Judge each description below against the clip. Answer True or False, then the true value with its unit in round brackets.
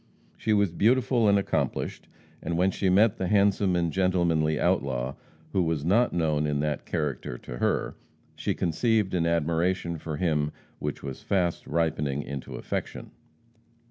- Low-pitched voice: True (85 Hz)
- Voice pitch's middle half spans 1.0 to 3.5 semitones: False (4.2 semitones)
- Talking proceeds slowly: False (150 wpm)